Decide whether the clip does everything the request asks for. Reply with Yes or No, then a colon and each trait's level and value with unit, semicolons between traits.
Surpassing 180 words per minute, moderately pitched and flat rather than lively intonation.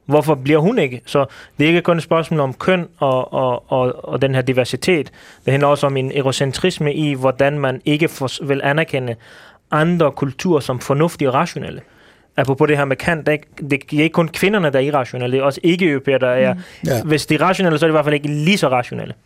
No: average, 220 wpm; medium, 145 Hz; average, 3.1 semitones